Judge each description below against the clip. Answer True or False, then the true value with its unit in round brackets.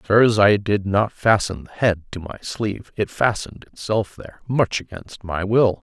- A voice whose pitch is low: True (105 Hz)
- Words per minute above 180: False (175 wpm)